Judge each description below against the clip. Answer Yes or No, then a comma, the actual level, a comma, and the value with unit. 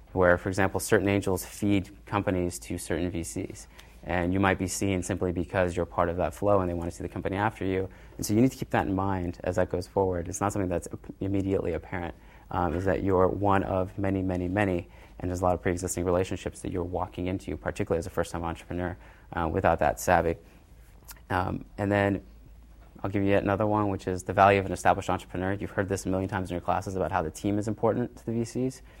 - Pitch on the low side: Yes, very low, 95 Hz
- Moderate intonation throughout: No, narrow, 1.9 semitones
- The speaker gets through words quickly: Yes, fast, 235 wpm